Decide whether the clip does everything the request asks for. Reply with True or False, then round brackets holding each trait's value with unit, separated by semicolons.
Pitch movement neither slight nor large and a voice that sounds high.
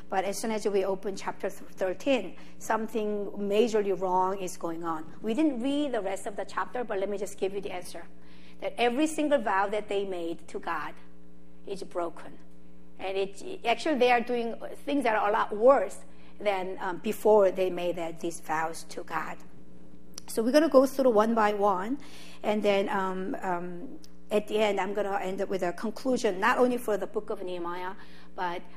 True (3.8 semitones; 195 Hz)